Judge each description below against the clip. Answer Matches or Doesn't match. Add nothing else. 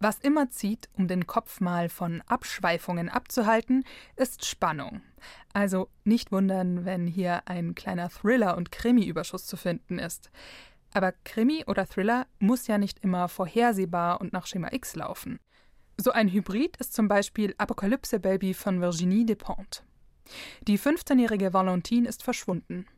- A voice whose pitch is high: Matches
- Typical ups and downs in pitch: Matches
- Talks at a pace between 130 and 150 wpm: Matches